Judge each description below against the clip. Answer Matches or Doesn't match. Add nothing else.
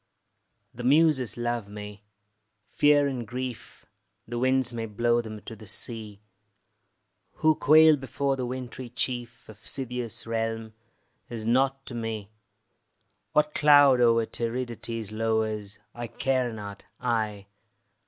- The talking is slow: Matches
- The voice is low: Matches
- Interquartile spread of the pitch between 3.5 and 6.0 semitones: Doesn't match